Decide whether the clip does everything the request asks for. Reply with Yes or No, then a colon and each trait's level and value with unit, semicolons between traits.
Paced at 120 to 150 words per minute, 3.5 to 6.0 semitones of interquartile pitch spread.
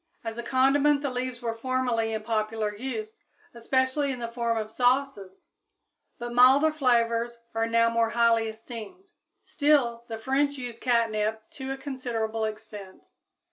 No: average, 145 wpm; average, 2.9 semitones